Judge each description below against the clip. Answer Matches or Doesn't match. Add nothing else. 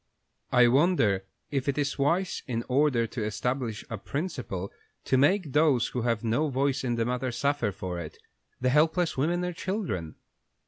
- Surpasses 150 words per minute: Matches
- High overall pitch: Doesn't match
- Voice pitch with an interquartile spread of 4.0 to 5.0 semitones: Matches